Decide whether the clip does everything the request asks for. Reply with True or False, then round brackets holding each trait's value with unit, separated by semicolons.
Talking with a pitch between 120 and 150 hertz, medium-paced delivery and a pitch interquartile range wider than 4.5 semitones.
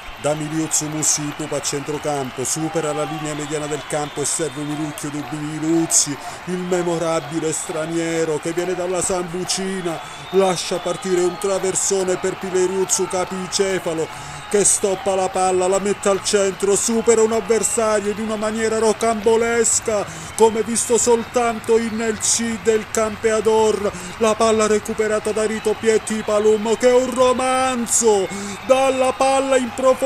False (190 Hz; 130 wpm; 5.2 semitones)